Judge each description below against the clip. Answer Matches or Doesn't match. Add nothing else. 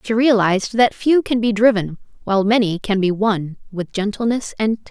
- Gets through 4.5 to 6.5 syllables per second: Matches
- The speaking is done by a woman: Matches